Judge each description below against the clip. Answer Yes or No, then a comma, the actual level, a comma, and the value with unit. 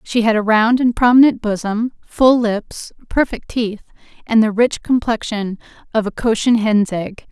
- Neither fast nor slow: Yes, average, 165 wpm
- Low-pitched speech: No, high, 225 Hz